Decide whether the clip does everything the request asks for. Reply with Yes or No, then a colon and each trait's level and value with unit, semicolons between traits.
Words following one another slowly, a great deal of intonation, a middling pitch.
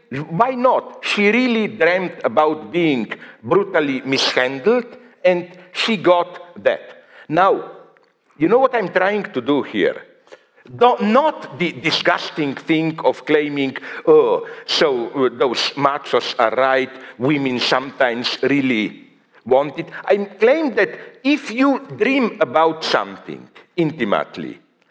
Yes: slow, 115 wpm; wide, 9.0 semitones; medium, 180 Hz